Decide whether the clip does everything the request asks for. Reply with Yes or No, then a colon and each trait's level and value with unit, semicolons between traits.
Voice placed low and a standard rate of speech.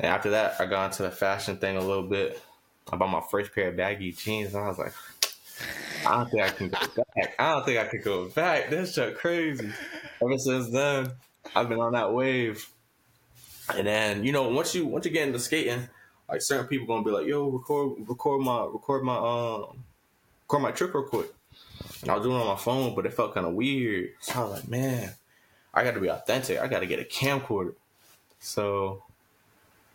No: low, 115 Hz; fast, 215 wpm